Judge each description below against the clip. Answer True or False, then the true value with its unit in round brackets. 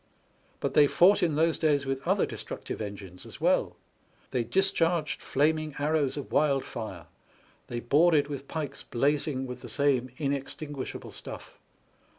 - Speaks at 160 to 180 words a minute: False (140 wpm)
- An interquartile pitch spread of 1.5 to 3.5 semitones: True (3.1 semitones)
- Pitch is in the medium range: True (145 Hz)